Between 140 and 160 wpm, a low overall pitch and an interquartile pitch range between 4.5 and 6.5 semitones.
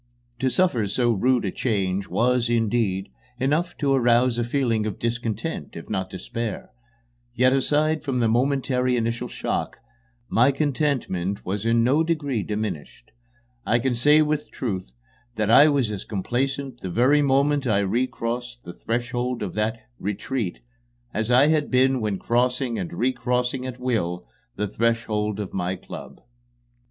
No: average, 150 wpm; low, 120 Hz; average, 3.7 semitones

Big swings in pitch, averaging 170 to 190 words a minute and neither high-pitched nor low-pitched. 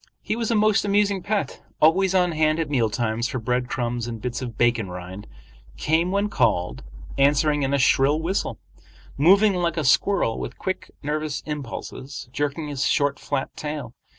Yes: wide, 6.4 semitones; average, 175 wpm; medium, 145 Hz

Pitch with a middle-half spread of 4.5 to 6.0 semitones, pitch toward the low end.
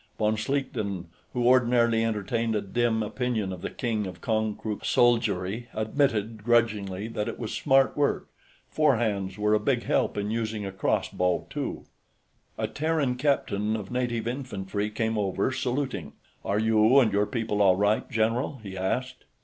No: average, 3.0 semitones; low, 110 Hz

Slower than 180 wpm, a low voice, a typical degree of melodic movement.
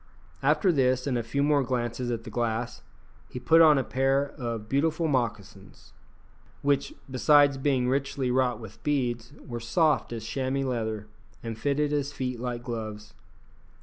Yes: average, 155 wpm; low, 125 Hz; average, 3.2 semitones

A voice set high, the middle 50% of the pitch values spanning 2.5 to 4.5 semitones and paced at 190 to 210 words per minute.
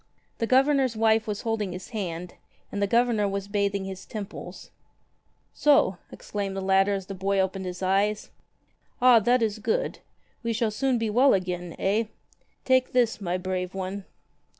No: high, 205 Hz; average, 3.1 semitones; average, 165 wpm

